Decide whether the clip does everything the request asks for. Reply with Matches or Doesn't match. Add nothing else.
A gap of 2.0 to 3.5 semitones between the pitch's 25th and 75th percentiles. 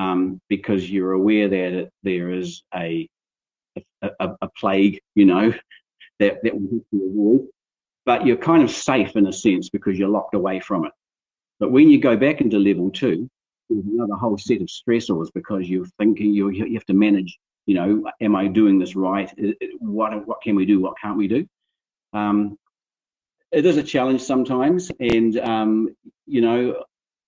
Matches